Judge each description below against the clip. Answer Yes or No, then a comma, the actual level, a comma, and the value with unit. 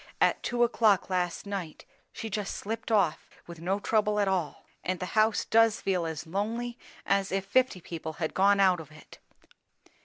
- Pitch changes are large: No, average, 3.6 semitones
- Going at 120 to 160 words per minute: No, average, 180 wpm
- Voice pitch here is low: No, high, 195 Hz